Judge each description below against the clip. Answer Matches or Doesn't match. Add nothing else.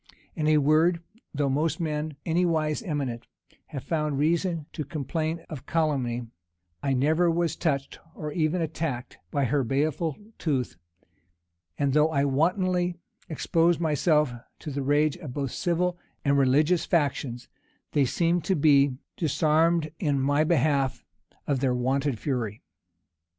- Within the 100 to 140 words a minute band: Matches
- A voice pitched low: Doesn't match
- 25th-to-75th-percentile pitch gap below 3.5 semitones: Matches